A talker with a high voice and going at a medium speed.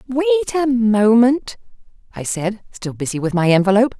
Yes: high, 230 Hz; average, 150 wpm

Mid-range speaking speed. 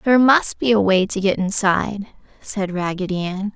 Yes: average, 185 wpm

